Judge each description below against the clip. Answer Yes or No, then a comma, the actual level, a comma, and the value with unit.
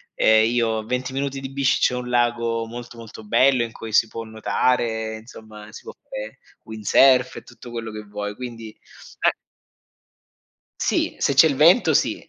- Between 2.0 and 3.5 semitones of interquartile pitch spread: Yes, narrow, 2.5 semitones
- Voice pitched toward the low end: Yes, low, 115 Hz